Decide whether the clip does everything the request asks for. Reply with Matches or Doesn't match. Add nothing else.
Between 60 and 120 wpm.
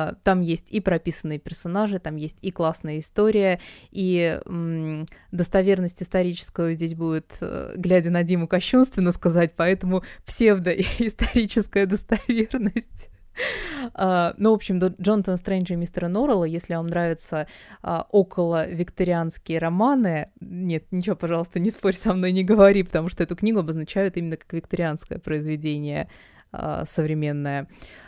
Doesn't match